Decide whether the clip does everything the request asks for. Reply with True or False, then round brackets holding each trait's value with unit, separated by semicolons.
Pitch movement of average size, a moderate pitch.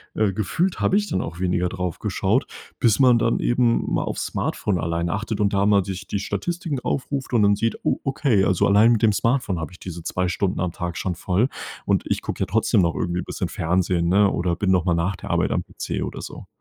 False (4.3 semitones; 100 Hz)